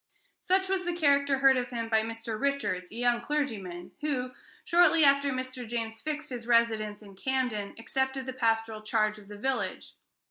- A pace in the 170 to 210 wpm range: Yes, average, 175 wpm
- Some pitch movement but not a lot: Yes, average, 4.0 semitones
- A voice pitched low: No, high, 245 Hz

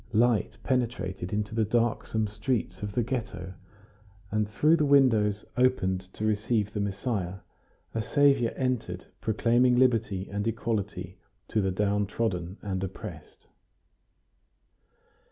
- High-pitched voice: No, low, 105 Hz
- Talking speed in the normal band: No, slow, 120 wpm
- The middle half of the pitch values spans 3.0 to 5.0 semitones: Yes, average, 3.6 semitones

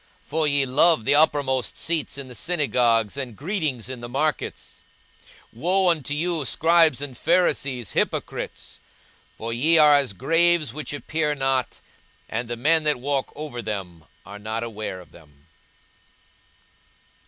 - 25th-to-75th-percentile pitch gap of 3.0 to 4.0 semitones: No, average, 4.8 semitones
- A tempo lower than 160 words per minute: Yes, average, 145 wpm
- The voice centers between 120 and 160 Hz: Yes, medium, 140 Hz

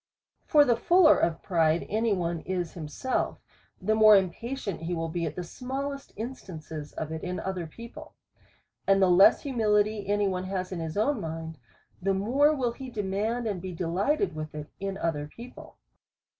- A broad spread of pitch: Yes, wide, 5.7 semitones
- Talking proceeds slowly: No, average, 180 wpm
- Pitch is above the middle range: Yes, high, 195 Hz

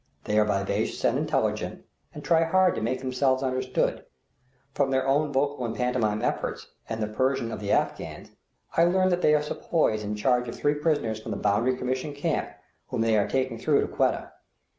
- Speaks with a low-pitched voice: Yes, low, 130 Hz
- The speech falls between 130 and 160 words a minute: No, average, 195 wpm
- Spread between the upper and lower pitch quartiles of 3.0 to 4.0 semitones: No, average, 4.6 semitones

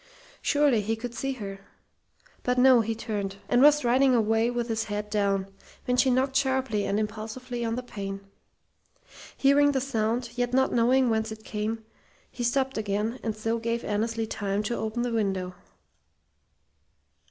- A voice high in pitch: Yes, high, 230 Hz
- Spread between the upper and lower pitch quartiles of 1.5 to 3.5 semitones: Yes, average, 2.9 semitones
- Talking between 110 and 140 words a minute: No, average, 165 wpm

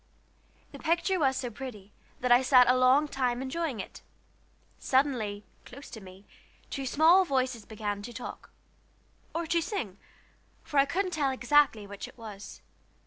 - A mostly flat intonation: No, average, 4.9 semitones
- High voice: Yes, very high, 255 Hz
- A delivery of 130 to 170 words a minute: Yes, average, 155 wpm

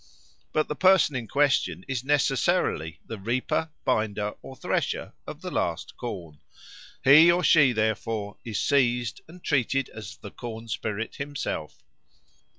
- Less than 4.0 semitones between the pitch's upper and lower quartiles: No, average, 5.0 semitones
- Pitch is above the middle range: No, low, 120 Hz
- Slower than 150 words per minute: Yes, average, 140 wpm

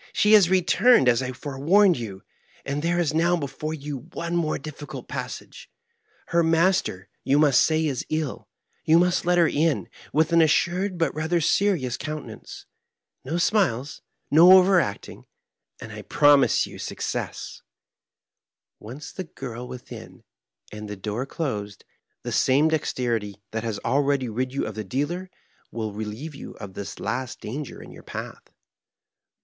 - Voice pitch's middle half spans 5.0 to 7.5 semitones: Yes, average, 5.3 semitones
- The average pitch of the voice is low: No, medium, 145 Hz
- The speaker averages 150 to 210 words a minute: Yes, average, 155 wpm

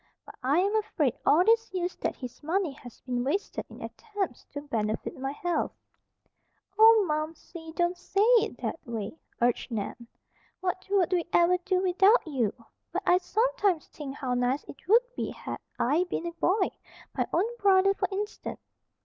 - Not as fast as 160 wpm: No, average, 170 wpm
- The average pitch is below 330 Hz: No, very high, 350 Hz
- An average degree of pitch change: No, wide, 6.1 semitones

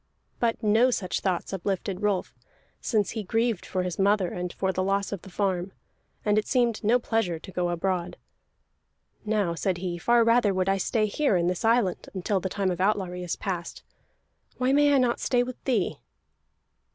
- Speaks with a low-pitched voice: No, high, 195 Hz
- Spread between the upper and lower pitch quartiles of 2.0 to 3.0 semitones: No, average, 3.8 semitones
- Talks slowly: No, average, 190 wpm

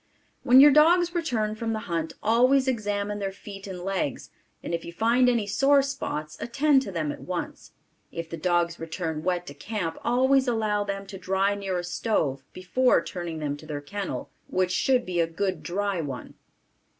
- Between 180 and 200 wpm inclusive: Yes, average, 185 wpm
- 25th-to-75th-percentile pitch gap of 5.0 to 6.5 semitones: Yes, wide, 5.6 semitones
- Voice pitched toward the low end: No, high, 195 Hz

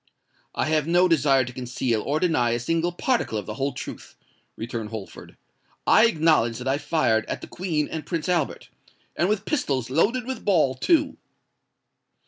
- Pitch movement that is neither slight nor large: No, wide, 5.9 semitones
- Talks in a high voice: No, medium, 150 Hz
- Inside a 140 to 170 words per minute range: Yes, average, 165 wpm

